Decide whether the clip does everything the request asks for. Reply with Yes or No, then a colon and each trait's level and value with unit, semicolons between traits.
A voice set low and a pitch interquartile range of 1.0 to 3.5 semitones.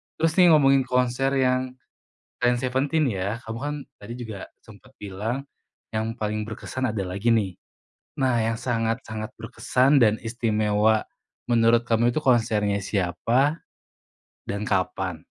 Yes: low, 115 Hz; average, 3.2 semitones